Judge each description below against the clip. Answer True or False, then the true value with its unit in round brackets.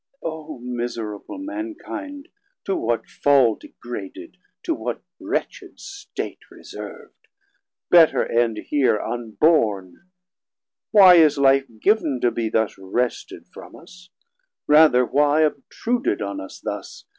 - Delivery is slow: True (115 wpm)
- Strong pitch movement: True (7.6 semitones)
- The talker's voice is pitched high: False (140 Hz)